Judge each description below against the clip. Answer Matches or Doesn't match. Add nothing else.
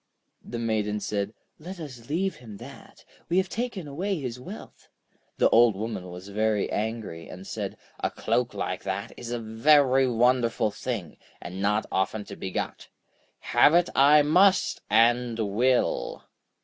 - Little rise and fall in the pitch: Doesn't match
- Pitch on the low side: Matches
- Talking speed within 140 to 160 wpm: Matches